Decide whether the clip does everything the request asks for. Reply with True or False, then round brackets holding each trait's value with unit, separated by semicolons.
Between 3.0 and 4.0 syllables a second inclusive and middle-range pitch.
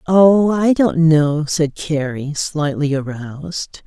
True (3.4 syllables/s; 155 Hz)